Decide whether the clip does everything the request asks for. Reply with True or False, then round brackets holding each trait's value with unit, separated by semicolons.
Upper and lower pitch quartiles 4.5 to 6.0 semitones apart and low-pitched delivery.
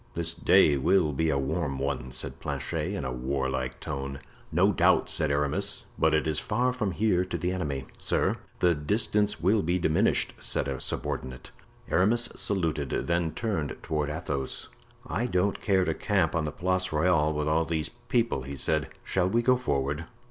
True (4.8 semitones; 80 Hz)